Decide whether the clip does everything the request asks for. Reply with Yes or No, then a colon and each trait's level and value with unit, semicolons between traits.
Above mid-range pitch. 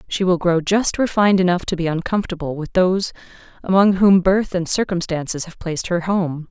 No: medium, 180 Hz